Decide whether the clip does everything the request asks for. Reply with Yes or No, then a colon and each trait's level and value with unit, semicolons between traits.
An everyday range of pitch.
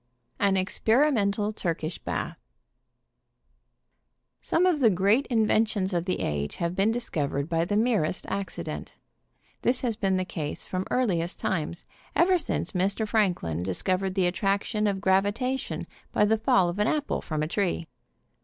Yes: average, 4.0 semitones